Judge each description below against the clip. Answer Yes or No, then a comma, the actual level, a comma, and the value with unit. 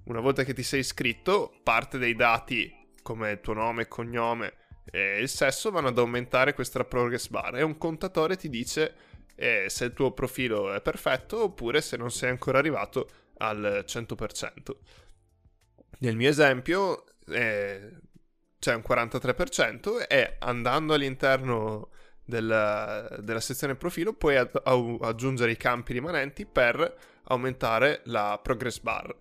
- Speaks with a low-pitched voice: Yes, low, 125 Hz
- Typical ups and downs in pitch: Yes, average, 3.2 semitones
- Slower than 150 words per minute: Yes, average, 140 wpm